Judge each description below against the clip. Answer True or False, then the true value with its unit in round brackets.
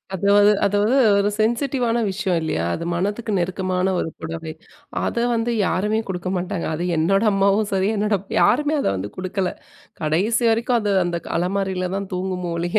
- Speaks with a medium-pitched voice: False (195 Hz)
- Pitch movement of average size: True (3.1 semitones)